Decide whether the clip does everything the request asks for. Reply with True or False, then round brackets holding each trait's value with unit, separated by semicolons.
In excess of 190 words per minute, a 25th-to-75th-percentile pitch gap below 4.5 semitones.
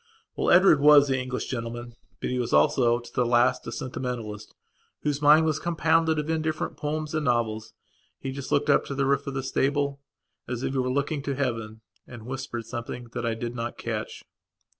True (200 wpm; 3.6 semitones)